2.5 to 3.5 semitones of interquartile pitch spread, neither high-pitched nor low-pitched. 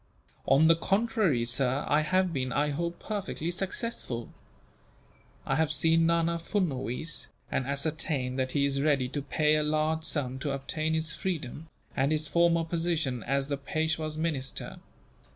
Yes: average, 3.2 semitones; medium, 155 Hz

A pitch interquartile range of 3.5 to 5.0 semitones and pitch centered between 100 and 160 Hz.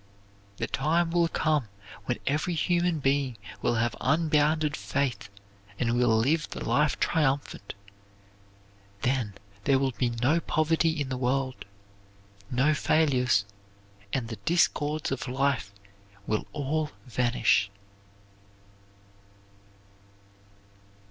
Yes: average, 4.0 semitones; medium, 140 Hz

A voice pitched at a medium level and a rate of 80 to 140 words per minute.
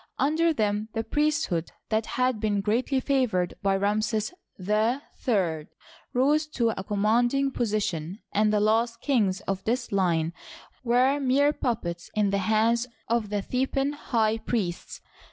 No: high, 220 Hz; slow, 135 wpm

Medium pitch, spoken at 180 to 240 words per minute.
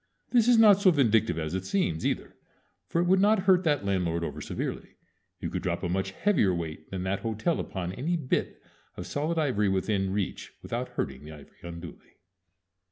No: low, 100 Hz; average, 190 wpm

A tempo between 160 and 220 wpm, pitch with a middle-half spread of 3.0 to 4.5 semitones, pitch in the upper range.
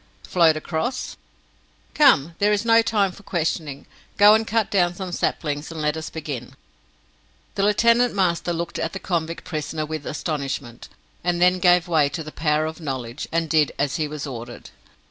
No: average, 175 wpm; average, 3.7 semitones; medium, 165 Hz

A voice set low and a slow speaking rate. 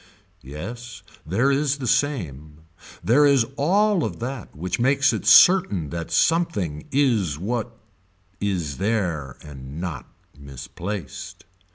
Yes: low, 105 Hz; slow, 115 wpm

